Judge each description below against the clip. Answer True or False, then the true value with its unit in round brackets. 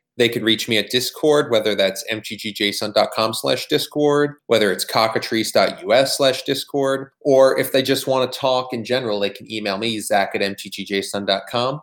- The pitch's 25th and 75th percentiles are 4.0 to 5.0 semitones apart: True (4.3 semitones)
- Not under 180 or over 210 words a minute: False (160 wpm)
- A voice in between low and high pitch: False (120 Hz)